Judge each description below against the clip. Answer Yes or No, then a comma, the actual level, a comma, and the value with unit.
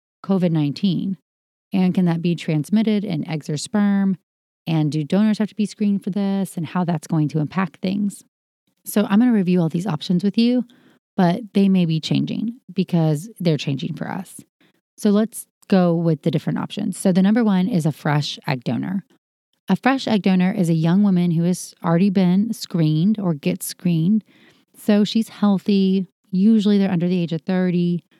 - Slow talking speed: No, average, 190 wpm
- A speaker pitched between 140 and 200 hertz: Yes, high, 190 Hz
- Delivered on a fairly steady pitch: No, average, 3.5 semitones